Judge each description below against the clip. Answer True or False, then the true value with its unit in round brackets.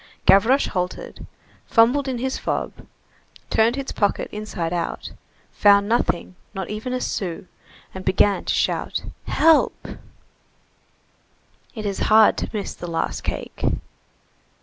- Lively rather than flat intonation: False (4.2 semitones)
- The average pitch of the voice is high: True (210 Hz)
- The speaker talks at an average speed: False (125 wpm)